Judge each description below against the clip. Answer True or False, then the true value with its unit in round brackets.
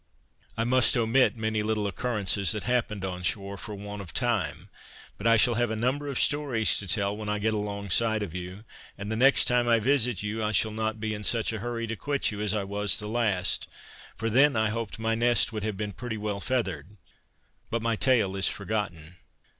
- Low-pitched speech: True (110 Hz)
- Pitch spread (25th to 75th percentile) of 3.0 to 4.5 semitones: False (2.4 semitones)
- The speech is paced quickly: True (215 wpm)